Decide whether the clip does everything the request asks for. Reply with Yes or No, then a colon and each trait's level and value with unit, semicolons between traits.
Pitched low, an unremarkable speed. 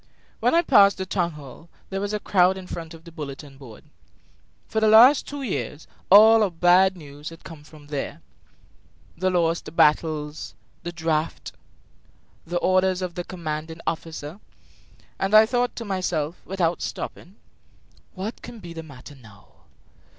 No: medium, 175 Hz; average, 160 wpm